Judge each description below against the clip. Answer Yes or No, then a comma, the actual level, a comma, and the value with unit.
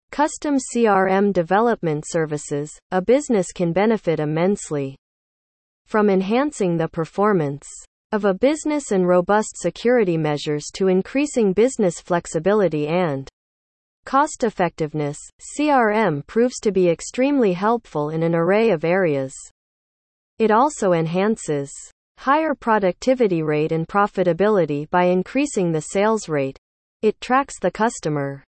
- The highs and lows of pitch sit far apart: Yes, wide, 5.9 semitones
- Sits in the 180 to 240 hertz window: Yes, medium, 185 Hz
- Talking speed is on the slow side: Yes, slow, 115 wpm